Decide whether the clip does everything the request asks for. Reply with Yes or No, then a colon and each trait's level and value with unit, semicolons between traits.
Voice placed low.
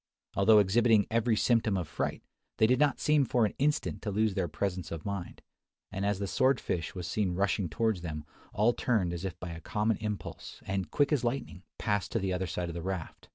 Yes: low, 100 Hz